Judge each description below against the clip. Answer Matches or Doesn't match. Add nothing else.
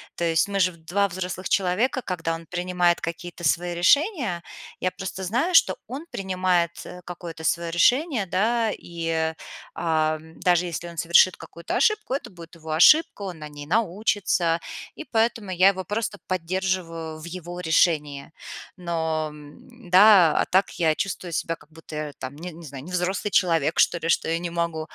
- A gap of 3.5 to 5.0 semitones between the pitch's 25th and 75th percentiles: Doesn't match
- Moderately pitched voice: Matches